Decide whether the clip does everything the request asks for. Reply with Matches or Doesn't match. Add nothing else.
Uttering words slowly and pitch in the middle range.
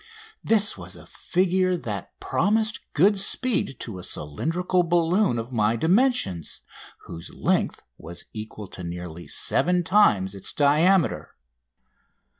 Matches